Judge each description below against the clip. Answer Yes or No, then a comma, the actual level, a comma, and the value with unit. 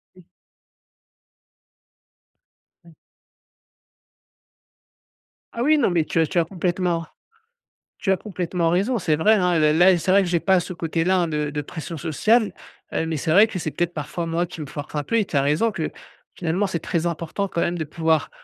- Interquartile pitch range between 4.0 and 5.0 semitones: No, average, 2.8 semitones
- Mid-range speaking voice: Yes, medium, 170 Hz